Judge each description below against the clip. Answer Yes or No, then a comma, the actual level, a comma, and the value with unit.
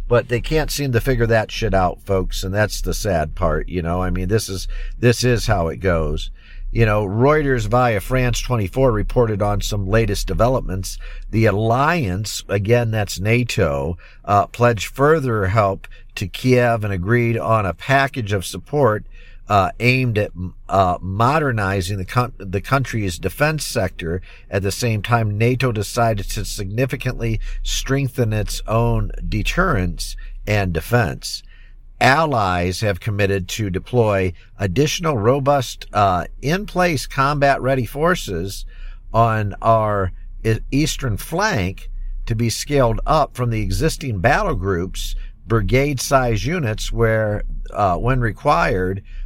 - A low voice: Yes, low, 110 Hz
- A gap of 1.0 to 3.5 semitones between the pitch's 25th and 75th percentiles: No, average, 4.3 semitones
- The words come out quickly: No, slow, 135 wpm